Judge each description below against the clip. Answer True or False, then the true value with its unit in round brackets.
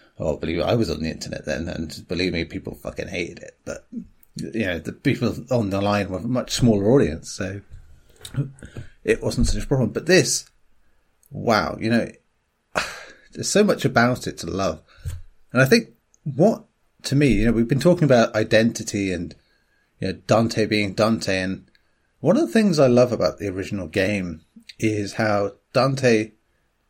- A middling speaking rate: True (180 wpm)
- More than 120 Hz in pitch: False (105 Hz)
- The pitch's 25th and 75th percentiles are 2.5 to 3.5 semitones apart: False (4.6 semitones)